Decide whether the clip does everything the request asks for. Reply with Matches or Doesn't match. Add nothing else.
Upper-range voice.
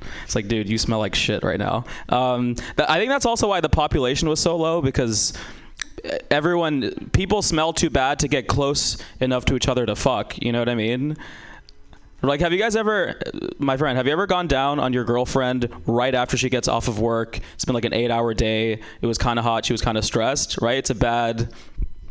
Doesn't match